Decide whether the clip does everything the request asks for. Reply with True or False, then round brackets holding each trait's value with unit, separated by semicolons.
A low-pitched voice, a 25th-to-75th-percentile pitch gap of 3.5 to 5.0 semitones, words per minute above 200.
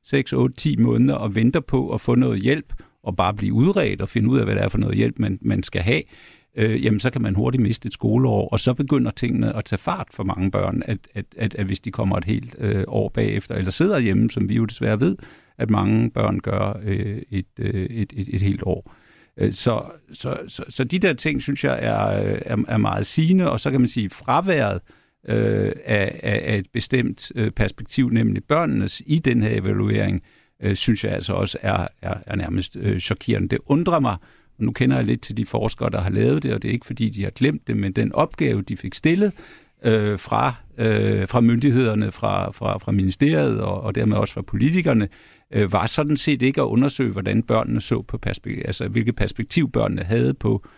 True (110 Hz; 3.9 semitones; 215 wpm)